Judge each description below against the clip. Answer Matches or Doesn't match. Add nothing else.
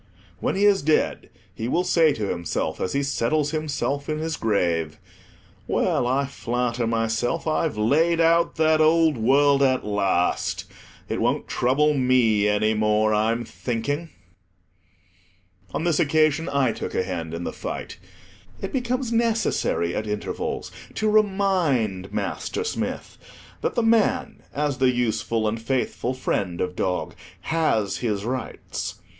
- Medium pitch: Doesn't match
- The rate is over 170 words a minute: Doesn't match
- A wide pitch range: Matches